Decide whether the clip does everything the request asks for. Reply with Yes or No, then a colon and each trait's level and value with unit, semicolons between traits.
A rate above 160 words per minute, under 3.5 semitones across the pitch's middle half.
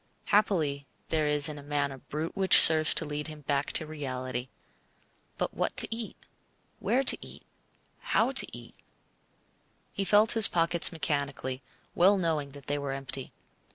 No: average, 155 wpm; average, 3.0 semitones